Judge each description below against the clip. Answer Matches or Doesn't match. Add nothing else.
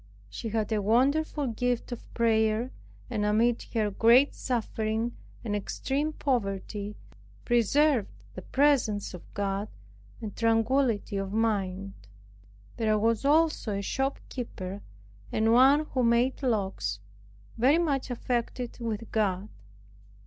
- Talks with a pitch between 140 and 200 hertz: Doesn't match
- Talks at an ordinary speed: Doesn't match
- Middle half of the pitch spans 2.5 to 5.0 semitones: Matches